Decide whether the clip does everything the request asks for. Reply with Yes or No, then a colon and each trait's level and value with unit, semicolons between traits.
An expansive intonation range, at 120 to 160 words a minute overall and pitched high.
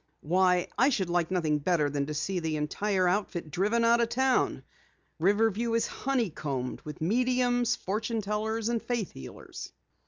Yes: wide, 6.1 semitones; average, 155 wpm; high, 195 Hz